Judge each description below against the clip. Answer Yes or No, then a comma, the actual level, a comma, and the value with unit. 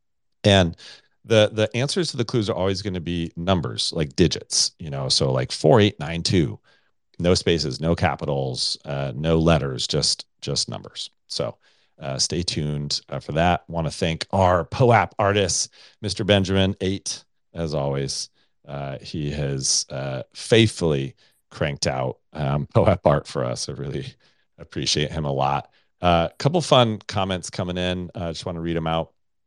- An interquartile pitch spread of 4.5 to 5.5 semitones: Yes, average, 5.1 semitones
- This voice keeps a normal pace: Yes, average, 165 wpm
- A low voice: Yes, very low, 85 Hz